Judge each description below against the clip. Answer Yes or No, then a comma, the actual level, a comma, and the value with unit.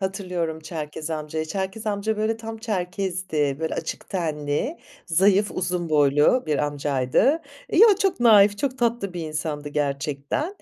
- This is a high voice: No, medium, 180 Hz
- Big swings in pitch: Yes, wide, 6.0 semitones